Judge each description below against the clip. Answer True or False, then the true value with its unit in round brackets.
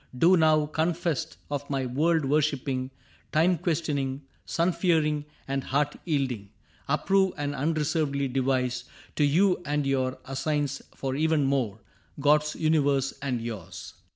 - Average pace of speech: False (125 wpm)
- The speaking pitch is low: False (145 Hz)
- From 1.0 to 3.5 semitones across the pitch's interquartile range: True (2.7 semitones)